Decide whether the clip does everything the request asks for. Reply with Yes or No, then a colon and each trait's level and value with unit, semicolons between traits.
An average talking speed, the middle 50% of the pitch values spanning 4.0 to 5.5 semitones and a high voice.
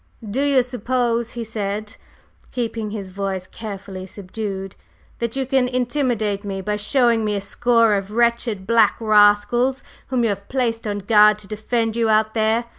No: average, 165 wpm; average, 2.7 semitones; high, 220 Hz